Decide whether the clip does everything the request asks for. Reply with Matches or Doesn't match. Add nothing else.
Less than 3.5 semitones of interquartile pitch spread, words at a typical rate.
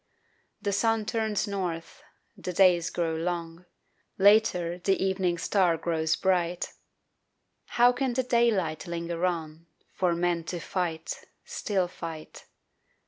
Doesn't match